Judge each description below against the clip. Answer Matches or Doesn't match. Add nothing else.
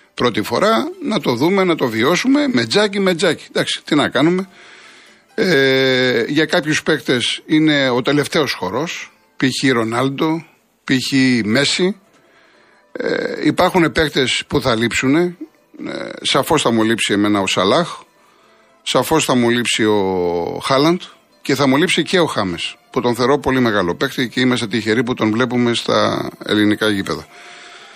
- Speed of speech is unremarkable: Matches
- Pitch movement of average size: Doesn't match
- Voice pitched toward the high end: Doesn't match